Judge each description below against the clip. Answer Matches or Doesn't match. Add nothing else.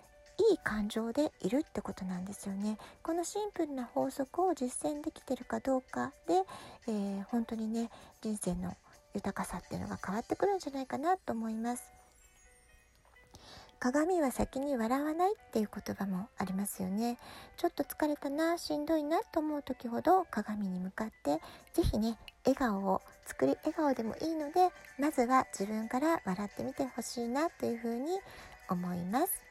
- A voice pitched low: Doesn't match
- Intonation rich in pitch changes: Matches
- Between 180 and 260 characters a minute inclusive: Doesn't match